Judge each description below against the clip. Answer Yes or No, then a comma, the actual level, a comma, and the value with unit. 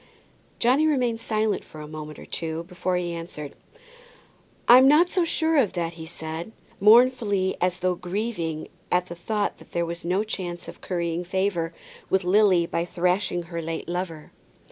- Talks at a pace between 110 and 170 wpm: Yes, average, 165 wpm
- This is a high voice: No, medium, 180 Hz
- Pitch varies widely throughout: No, average, 4.1 semitones